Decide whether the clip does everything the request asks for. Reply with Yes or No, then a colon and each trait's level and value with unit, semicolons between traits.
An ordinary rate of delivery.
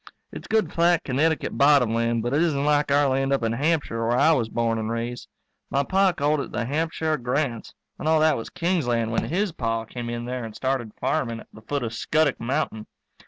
No: fast, 220 wpm